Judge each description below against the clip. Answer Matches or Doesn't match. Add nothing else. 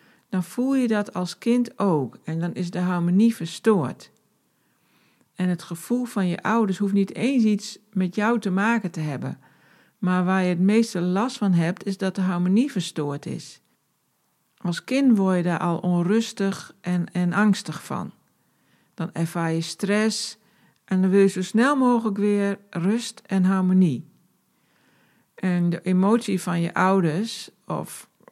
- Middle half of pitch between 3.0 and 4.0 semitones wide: Matches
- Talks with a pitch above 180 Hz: Matches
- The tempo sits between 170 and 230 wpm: Doesn't match